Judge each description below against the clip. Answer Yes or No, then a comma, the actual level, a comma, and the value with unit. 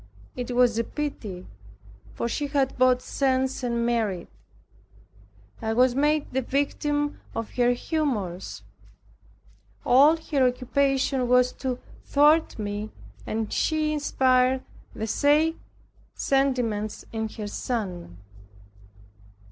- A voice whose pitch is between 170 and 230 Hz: No, very high, 255 Hz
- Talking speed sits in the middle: No, slow, 110 wpm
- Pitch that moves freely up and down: No, average, 3.8 semitones